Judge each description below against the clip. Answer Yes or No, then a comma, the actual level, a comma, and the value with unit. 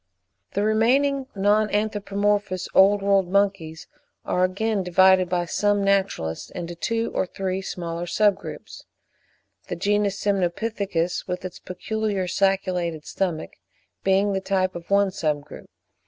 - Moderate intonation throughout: No, narrow, 2.3 semitones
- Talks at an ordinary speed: No, slow, 130 wpm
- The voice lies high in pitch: Yes, high, 195 Hz